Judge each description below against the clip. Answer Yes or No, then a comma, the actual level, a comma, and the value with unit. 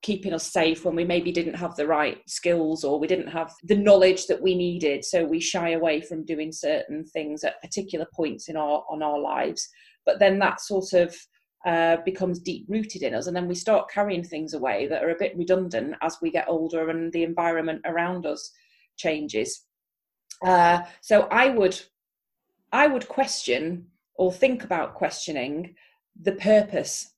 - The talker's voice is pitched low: No, medium, 175 Hz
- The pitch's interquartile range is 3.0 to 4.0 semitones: Yes, average, 3.4 semitones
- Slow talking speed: No, average, 180 wpm